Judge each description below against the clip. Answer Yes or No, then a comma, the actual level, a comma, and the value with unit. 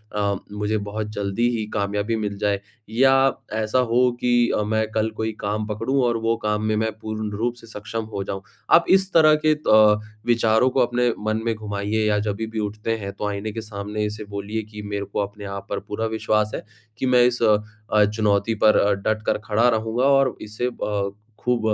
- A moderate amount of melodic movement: No, narrow, 1.8 semitones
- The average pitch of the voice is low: Yes, low, 110 Hz